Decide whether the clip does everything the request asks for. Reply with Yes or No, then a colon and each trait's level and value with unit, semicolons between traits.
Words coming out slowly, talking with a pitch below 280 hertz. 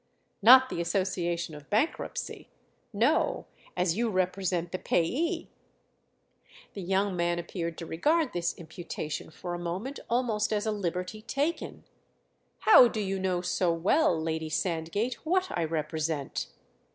Yes: slow, 130 wpm; medium, 185 Hz